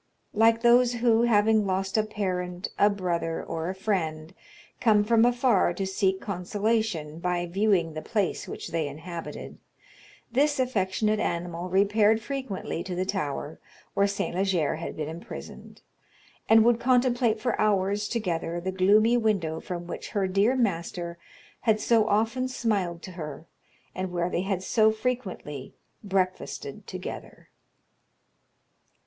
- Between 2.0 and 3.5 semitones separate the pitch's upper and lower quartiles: No, average, 4.1 semitones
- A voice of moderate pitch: No, high, 195 Hz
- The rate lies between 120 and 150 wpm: Yes, average, 140 wpm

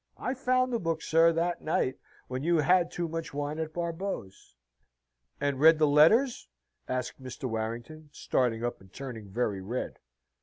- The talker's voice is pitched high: No, medium, 150 Hz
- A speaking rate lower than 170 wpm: Yes, average, 160 wpm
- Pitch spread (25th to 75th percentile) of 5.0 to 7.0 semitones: Yes, average, 5.3 semitones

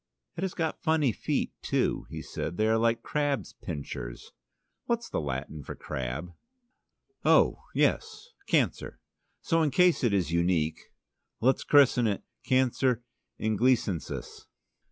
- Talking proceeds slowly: Yes, slow, 130 wpm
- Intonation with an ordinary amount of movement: No, wide, 9.0 semitones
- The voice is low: Yes, low, 115 Hz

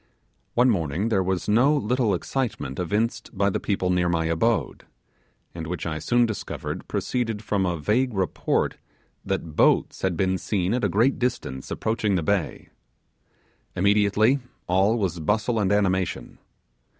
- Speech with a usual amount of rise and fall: Yes, average, 4.2 semitones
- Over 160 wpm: No, average, 150 wpm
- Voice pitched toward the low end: Yes, low, 100 Hz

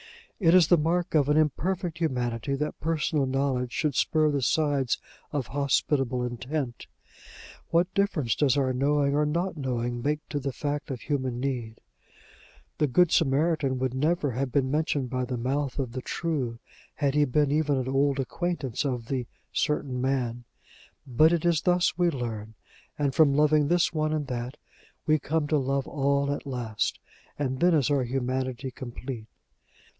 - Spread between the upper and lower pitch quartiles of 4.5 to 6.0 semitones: No, average, 3.1 semitones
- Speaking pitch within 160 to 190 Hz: No, medium, 140 Hz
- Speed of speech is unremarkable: Yes, average, 170 wpm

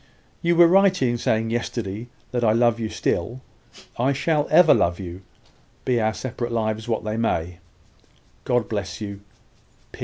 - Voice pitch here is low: Yes, low, 115 Hz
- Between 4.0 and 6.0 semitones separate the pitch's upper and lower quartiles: No, average, 3.0 semitones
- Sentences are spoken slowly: No, average, 155 wpm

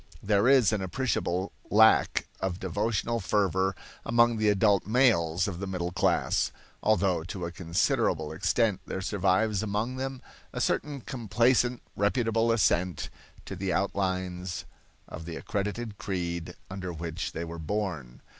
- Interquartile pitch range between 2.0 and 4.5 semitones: Yes, average, 3.9 semitones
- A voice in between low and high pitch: No, low, 100 Hz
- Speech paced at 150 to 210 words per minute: No, slow, 135 wpm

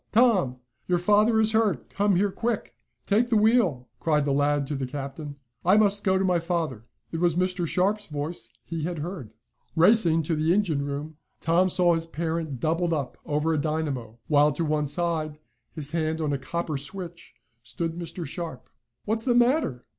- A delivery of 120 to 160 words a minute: No, average, 185 wpm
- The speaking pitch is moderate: Yes, medium, 165 Hz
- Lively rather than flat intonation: No, average, 4.2 semitones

